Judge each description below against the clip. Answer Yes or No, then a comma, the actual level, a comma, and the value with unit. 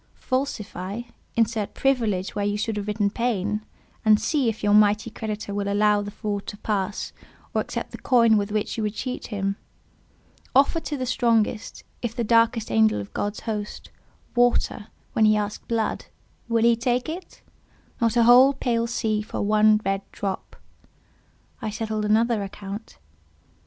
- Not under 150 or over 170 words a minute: Yes, average, 155 wpm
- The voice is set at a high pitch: Yes, high, 215 Hz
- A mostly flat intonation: Yes, narrow, 2.2 semitones